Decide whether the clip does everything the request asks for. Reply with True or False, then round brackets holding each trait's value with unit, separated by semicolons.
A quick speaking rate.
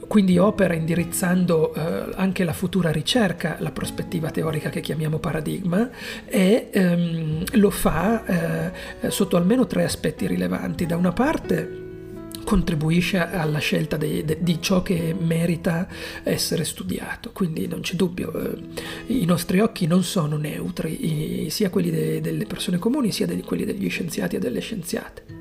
False (130 wpm)